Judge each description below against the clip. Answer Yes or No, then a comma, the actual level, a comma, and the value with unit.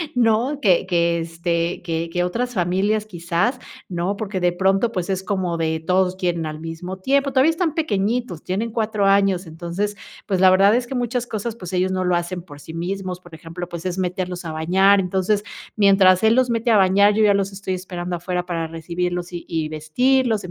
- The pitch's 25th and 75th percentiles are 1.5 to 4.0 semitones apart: Yes, average, 3.3 semitones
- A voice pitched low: No, medium, 185 Hz